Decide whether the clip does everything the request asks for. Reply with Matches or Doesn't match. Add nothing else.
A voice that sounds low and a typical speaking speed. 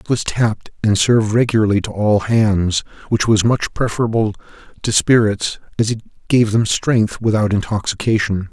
Matches